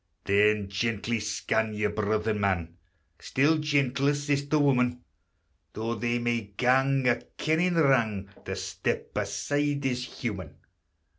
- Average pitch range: Yes, average, 4.8 semitones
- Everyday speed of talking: No, slow, 120 wpm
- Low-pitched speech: Yes, low, 120 Hz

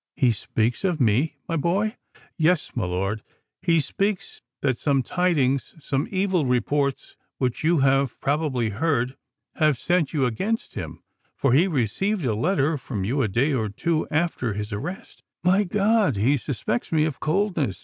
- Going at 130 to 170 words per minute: Yes, average, 150 wpm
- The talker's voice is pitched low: No, medium, 145 Hz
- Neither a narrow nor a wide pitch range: No, wide, 6.0 semitones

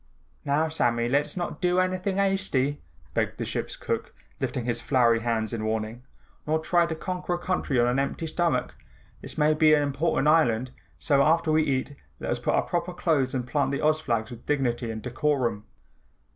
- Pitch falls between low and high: Yes, medium, 145 Hz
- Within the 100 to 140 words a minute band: No, average, 195 wpm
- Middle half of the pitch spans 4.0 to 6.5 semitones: Yes, average, 5.1 semitones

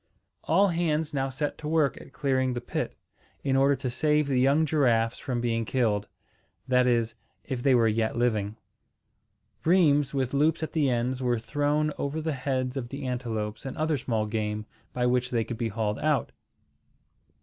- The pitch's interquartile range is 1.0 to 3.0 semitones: No, average, 3.7 semitones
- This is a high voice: No, low, 130 Hz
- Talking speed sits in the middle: Yes, average, 180 wpm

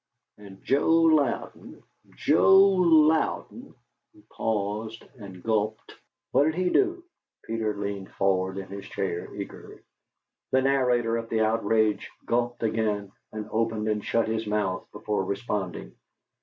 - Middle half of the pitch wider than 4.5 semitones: No, average, 3.4 semitones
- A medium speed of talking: No, slow, 130 wpm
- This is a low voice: Yes, low, 110 Hz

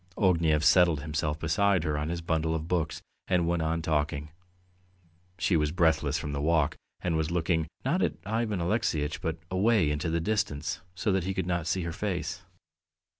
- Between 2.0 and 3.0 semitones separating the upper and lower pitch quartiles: Yes, average, 2.7 semitones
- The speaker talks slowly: No, average, 180 wpm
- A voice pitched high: No, very low, 80 Hz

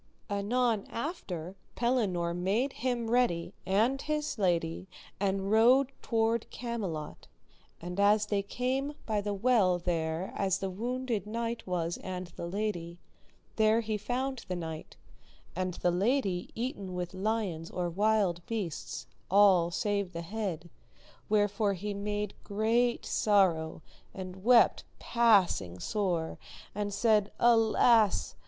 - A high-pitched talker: Yes, high, 205 Hz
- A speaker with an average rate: No, slow, 125 wpm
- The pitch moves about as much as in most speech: Yes, average, 4.1 semitones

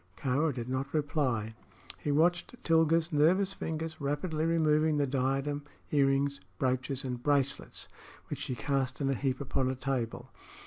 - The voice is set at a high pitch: No, medium, 140 Hz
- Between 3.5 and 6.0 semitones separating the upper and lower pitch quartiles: No, average, 3.0 semitones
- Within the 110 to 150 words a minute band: Yes, average, 145 wpm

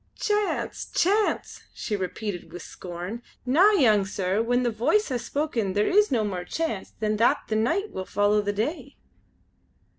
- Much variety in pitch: Yes, wide, 6.8 semitones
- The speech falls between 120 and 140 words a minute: No, average, 160 wpm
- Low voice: No, high, 220 Hz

